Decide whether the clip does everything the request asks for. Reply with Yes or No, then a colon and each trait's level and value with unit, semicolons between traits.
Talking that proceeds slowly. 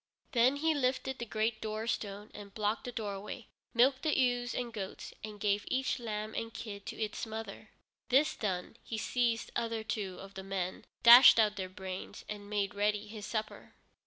No: average, 180 wpm